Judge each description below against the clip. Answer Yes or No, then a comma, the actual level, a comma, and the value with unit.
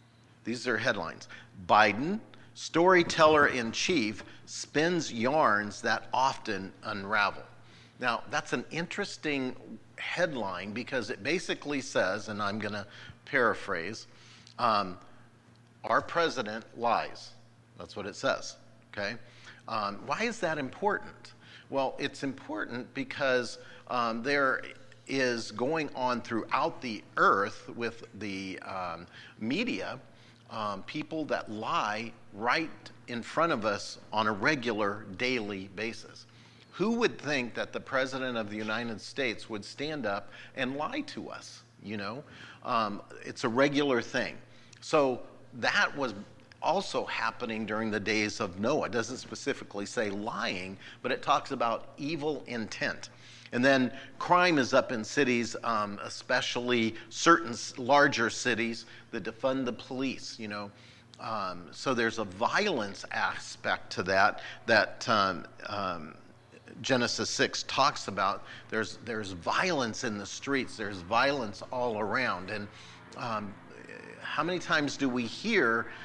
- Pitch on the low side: Yes, low, 120 Hz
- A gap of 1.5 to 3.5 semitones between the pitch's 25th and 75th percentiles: Yes, average, 3.1 semitones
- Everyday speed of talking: No, slow, 130 wpm